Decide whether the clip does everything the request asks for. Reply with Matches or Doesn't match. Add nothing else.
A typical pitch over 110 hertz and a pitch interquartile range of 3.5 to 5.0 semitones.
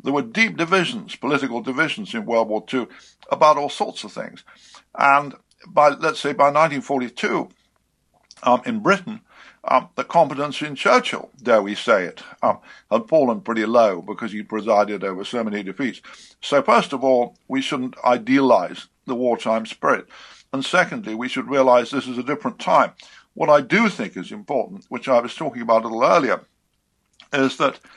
Matches